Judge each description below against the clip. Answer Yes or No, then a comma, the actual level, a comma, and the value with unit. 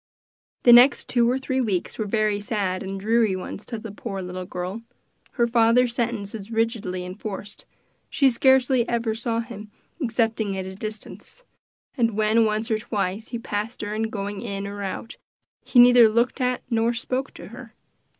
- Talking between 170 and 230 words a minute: Yes, average, 175 wpm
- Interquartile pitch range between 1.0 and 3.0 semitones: Yes, average, 2.7 semitones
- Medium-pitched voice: No, high, 225 Hz